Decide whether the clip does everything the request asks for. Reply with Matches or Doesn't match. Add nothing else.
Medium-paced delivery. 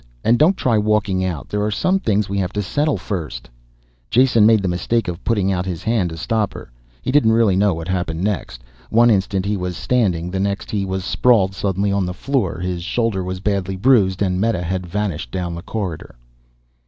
Doesn't match